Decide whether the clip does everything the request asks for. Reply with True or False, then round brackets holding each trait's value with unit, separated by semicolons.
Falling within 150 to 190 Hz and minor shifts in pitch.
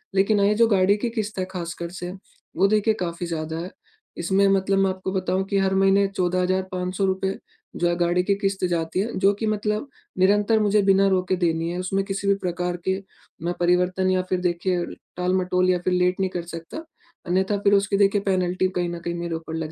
True (185 Hz; 1.8 semitones)